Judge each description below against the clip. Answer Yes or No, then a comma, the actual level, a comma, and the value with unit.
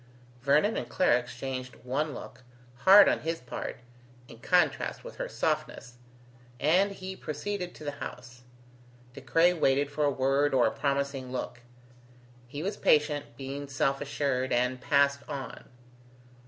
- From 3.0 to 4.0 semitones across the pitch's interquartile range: Yes, average, 3.3 semitones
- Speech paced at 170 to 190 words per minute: No, average, 145 wpm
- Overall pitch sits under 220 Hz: Yes, medium, 140 Hz